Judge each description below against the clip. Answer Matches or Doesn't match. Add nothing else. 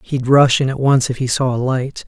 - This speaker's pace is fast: Matches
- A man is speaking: Matches